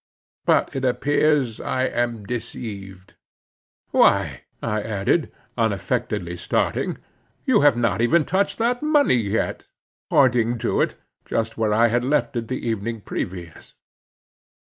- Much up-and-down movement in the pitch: No, average, 3.9 semitones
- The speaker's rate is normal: No, slow, 125 wpm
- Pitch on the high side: No, low, 115 Hz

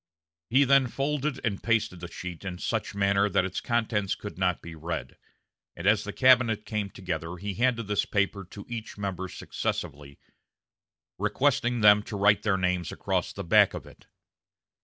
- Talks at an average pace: Yes, average, 170 wpm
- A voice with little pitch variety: No, average, 3.9 semitones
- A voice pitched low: Yes, low, 100 Hz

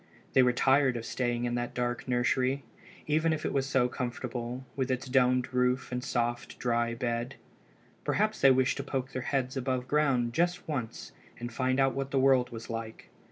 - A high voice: No, low, 125 Hz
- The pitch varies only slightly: Yes, narrow, 1.8 semitones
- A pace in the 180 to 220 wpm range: Yes, average, 190 wpm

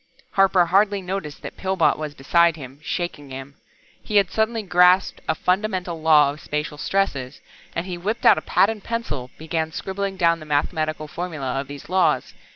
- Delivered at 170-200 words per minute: Yes, average, 175 wpm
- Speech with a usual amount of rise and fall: Yes, average, 4.3 semitones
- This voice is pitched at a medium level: Yes, medium, 170 Hz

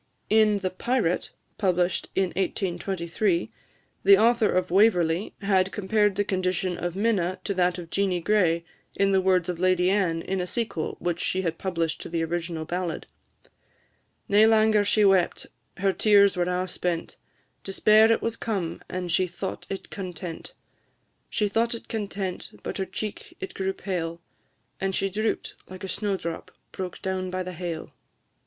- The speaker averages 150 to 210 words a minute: Yes, average, 160 wpm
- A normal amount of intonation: No, narrow, 2.3 semitones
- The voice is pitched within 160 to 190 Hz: Yes, medium, 185 Hz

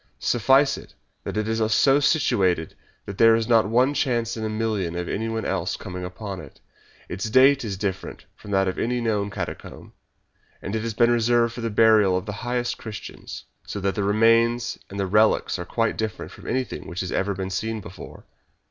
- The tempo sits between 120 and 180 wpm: No, average, 200 wpm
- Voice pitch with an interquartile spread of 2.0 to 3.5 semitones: Yes, average, 3.1 semitones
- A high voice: No, low, 110 Hz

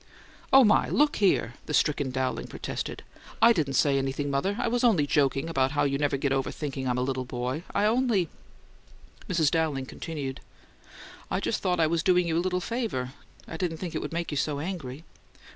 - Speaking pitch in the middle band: Yes, medium, 155 Hz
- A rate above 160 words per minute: Yes, fast, 205 wpm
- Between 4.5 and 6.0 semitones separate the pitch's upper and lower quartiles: Yes, average, 5.1 semitones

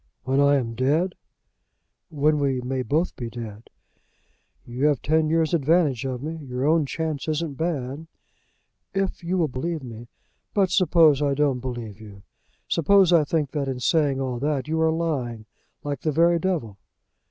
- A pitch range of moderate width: Yes, average, 4.2 semitones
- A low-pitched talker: No, medium, 145 Hz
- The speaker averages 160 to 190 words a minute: Yes, average, 170 wpm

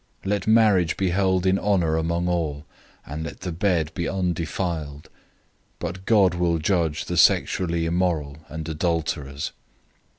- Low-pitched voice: Yes, very low, 85 Hz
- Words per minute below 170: Yes, average, 140 wpm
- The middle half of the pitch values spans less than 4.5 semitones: Yes, average, 2.7 semitones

